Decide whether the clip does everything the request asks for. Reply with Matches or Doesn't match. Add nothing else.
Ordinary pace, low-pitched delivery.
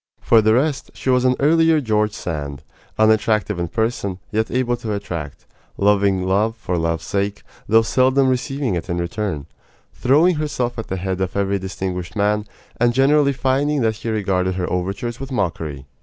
Matches